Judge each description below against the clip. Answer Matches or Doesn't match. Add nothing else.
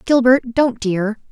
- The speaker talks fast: Doesn't match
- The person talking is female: Matches